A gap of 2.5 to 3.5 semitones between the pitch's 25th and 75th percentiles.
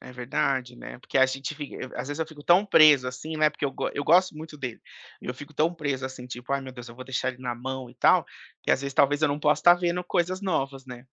Yes: average, 3.2 semitones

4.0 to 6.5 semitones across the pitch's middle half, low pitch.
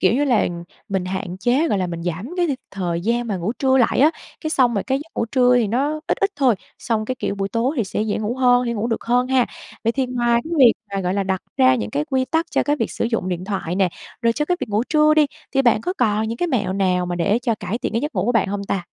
No: average, 5.1 semitones; high, 230 Hz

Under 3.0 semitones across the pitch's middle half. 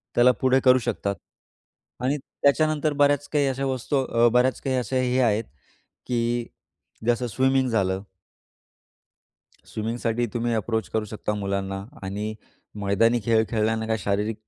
No: average, 3.4 semitones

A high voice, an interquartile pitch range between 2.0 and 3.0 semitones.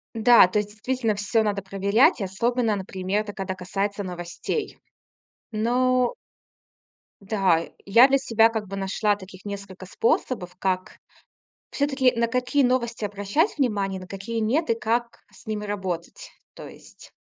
No: high, 210 Hz; average, 3.6 semitones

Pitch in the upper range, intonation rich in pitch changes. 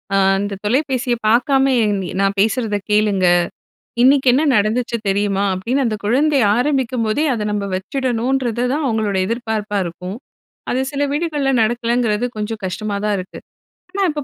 No: high, 230 Hz; average, 4.2 semitones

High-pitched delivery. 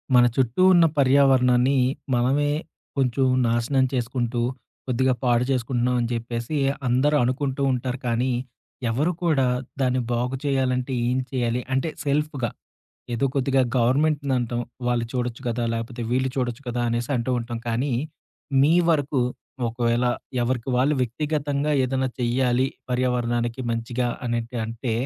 No: low, 125 Hz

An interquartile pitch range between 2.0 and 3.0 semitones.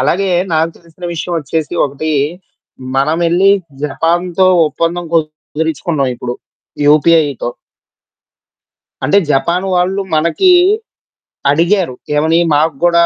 Yes: average, 2.7 semitones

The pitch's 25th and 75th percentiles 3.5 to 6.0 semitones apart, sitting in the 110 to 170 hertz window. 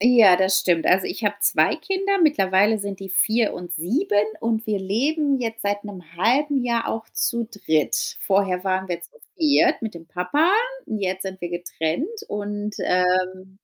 No: average, 3.9 semitones; high, 205 Hz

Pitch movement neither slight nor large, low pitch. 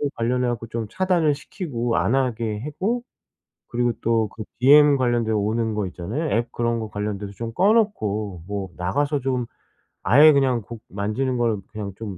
Yes: average, 4.2 semitones; low, 115 Hz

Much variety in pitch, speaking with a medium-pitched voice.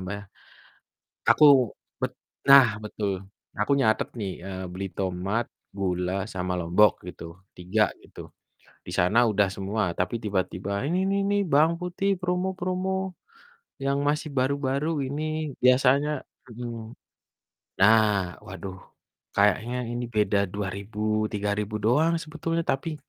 No: wide, 6.6 semitones; low, 110 Hz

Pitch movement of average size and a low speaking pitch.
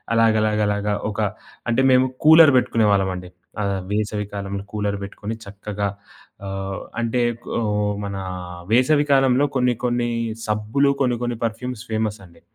Yes: average, 3.4 semitones; low, 110 Hz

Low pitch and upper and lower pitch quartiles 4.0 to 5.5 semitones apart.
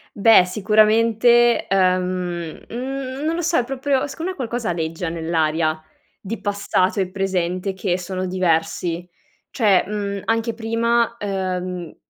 No: high, 195 Hz; average, 4.4 semitones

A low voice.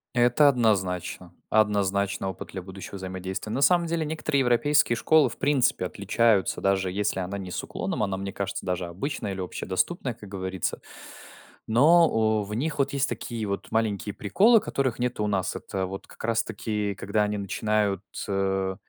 Yes: low, 105 Hz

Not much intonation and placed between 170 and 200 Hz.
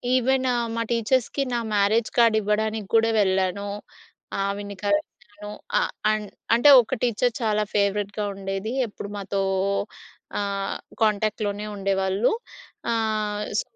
No: narrow, 1.9 semitones; high, 210 Hz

